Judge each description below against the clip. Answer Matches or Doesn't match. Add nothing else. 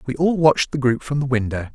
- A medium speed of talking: Doesn't match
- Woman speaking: Doesn't match